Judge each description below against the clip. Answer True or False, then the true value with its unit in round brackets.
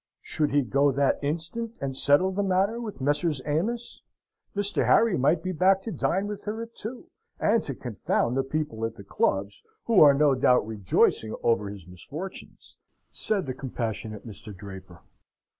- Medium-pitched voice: True (145 Hz)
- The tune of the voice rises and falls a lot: True (9.0 semitones)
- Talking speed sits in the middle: True (170 wpm)